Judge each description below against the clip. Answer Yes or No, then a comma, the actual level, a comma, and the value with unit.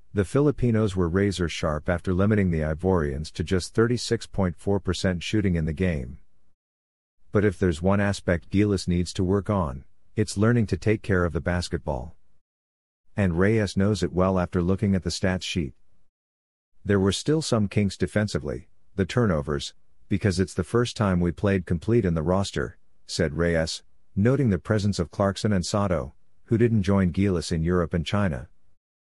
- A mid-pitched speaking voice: No, very low, 95 Hz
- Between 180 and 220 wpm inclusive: No, average, 165 wpm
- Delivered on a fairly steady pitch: No, average, 3.2 semitones